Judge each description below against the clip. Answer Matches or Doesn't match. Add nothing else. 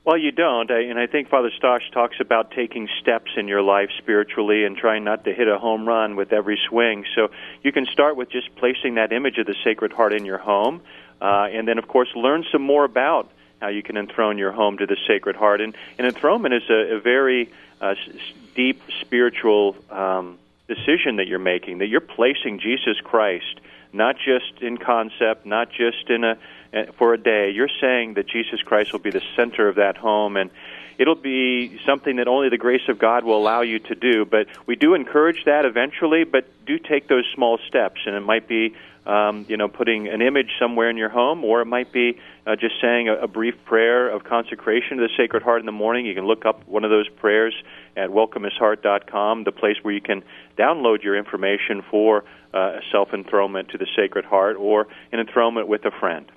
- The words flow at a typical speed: Doesn't match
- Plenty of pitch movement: Doesn't match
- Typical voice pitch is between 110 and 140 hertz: Matches